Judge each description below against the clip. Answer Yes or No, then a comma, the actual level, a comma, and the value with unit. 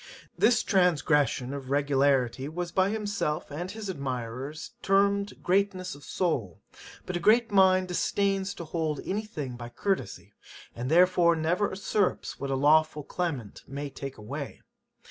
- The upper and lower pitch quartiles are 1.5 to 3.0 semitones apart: No, wide, 5.6 semitones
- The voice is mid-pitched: Yes, medium, 165 Hz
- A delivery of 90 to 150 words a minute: Yes, average, 145 wpm